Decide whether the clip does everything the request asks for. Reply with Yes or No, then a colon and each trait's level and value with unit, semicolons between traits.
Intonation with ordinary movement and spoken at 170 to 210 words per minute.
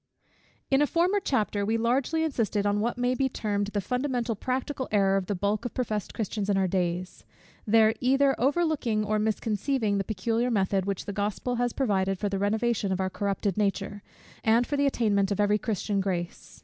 Yes: average, 3.7 semitones; average, 195 wpm